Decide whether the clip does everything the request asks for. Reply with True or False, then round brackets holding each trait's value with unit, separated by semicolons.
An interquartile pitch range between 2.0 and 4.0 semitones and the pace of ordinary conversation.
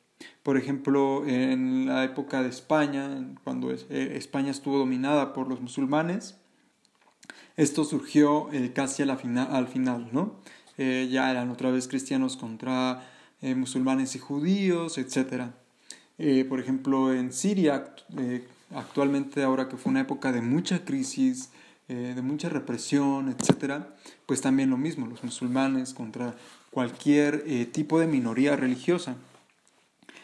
False (2.7 semitones; 115 wpm)